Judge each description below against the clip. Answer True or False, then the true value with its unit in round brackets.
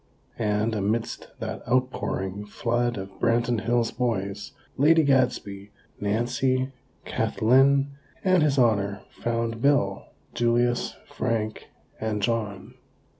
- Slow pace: True (100 wpm)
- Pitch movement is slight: False (3.5 semitones)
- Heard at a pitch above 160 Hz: False (115 Hz)